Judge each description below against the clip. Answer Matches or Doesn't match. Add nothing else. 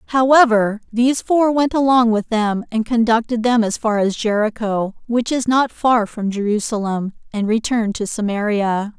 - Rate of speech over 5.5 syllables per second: Doesn't match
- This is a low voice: Doesn't match